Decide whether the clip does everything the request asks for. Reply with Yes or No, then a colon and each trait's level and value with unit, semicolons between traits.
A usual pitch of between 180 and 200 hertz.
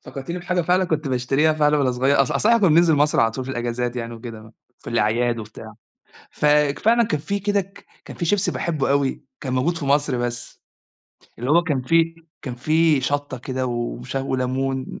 No: medium, 140 Hz